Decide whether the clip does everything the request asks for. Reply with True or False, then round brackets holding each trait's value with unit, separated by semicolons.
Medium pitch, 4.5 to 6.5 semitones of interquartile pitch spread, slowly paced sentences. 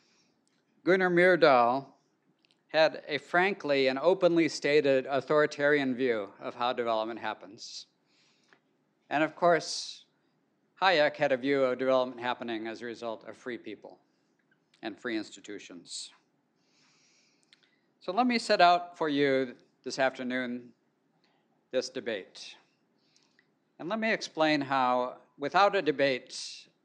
True (145 Hz; 5.4 semitones; 115 wpm)